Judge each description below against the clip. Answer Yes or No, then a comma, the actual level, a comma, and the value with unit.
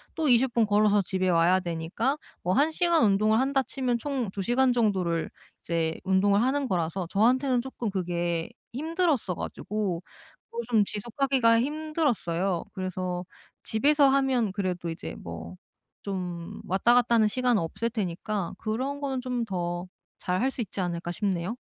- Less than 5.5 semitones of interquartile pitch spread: No, wide, 6.1 semitones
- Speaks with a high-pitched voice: Yes, high, 215 Hz